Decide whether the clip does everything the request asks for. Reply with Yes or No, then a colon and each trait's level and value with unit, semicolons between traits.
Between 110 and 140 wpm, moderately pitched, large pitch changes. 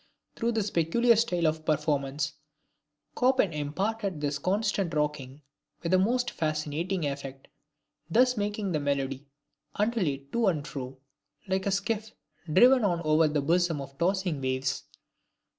Yes: slow, 135 wpm; medium, 165 Hz; wide, 6.0 semitones